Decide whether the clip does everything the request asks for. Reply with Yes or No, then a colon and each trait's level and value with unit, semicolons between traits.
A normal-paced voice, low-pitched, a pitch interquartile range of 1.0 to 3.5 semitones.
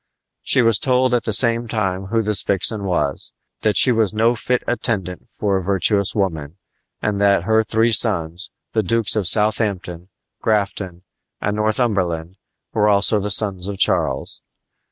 Yes: average, 155 wpm; low, 105 Hz; average, 2.8 semitones